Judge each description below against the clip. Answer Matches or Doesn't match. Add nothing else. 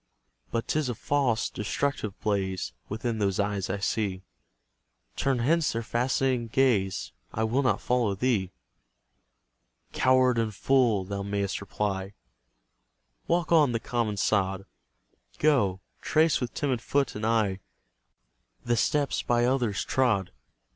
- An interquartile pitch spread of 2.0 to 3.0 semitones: Doesn't match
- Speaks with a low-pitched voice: Matches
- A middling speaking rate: Doesn't match